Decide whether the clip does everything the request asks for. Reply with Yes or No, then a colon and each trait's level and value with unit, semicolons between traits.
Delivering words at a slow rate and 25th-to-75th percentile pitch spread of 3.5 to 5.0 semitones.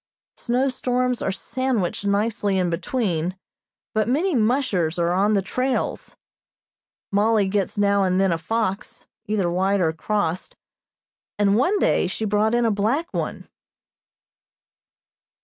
Yes: slow, 130 wpm; average, 4.1 semitones